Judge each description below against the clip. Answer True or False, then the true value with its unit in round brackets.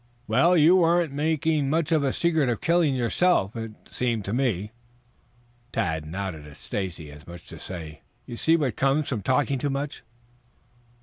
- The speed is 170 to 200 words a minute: True (180 wpm)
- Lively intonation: True (7.9 semitones)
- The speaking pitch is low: True (130 Hz)